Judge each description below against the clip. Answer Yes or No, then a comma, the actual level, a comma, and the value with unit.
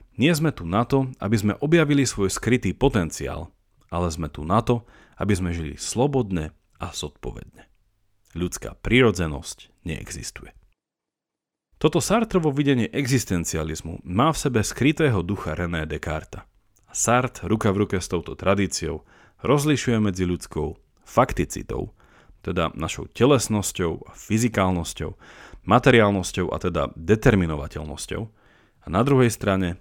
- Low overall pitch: Yes, low, 100 Hz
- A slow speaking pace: No, average, 120 wpm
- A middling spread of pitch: No, wide, 6.0 semitones